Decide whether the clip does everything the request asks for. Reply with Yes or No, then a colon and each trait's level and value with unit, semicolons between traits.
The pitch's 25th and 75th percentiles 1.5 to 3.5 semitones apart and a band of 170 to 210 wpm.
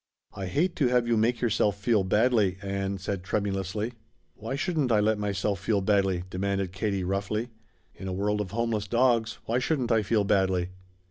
Yes: average, 3.1 semitones; average, 180 wpm